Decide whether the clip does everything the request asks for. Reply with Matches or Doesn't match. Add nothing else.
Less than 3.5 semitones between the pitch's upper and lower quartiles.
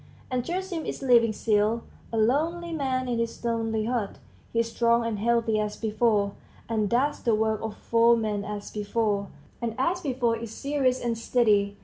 Matches